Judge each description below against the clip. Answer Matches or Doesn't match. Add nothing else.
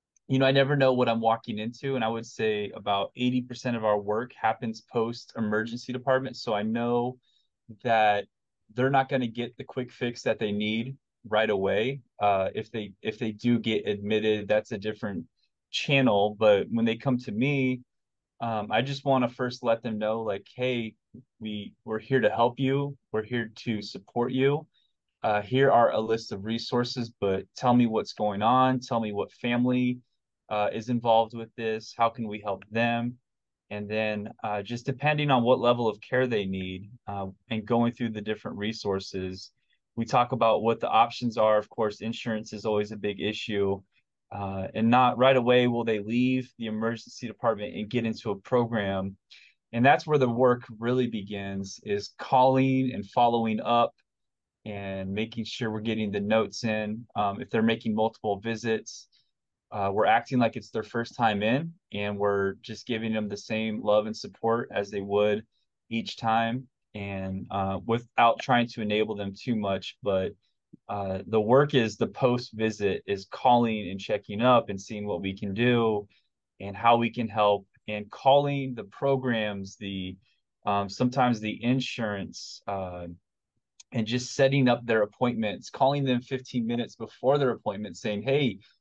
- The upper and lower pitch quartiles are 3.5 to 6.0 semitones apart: Doesn't match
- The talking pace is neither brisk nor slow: Matches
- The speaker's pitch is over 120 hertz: Doesn't match